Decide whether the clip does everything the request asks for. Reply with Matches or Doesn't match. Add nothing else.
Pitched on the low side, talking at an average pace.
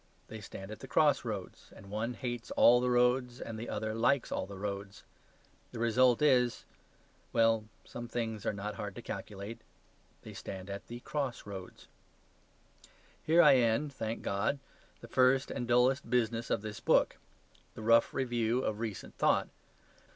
Matches